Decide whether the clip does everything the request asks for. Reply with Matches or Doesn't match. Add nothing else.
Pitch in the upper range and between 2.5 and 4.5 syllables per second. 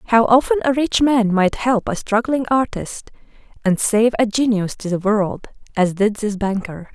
Matches